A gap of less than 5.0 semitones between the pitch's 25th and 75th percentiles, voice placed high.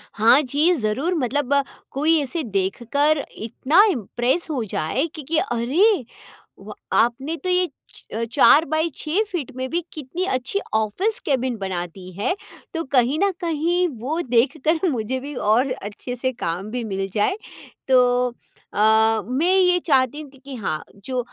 No: wide, 5.4 semitones; very high, 265 Hz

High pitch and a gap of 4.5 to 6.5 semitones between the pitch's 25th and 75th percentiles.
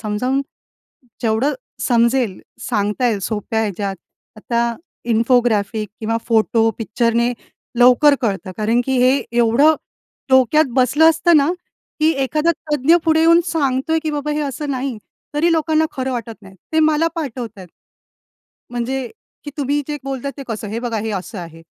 Yes: very high, 250 Hz; average, 4.9 semitones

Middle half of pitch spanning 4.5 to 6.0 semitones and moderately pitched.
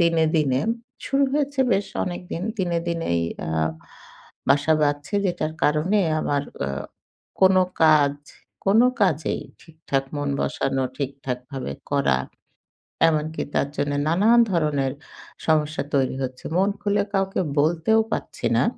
Yes: average, 4.8 semitones; medium, 155 Hz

